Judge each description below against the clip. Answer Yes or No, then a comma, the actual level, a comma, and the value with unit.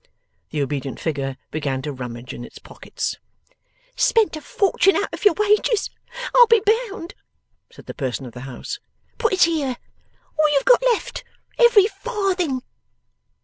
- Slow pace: No, average, 150 wpm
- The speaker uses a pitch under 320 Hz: No, very high, 330 Hz